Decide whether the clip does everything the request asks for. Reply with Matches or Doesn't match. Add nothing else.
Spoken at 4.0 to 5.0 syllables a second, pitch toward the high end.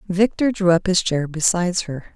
Doesn't match